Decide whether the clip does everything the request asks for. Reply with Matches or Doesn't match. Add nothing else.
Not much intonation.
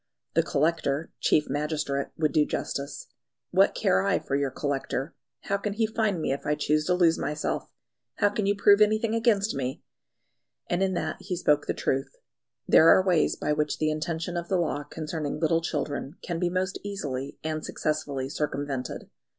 Doesn't match